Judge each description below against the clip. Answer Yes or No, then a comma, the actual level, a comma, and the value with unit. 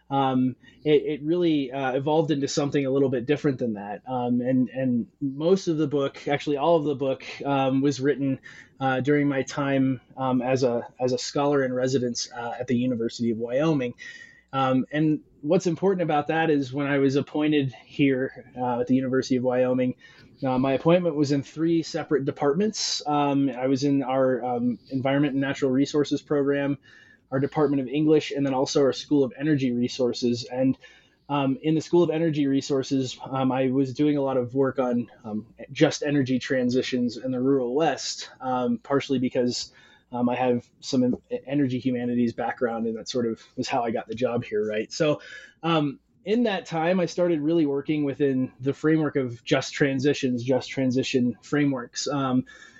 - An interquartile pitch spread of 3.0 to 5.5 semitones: No, narrow, 2.5 semitones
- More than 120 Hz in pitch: Yes, low, 135 Hz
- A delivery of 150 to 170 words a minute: No, average, 185 wpm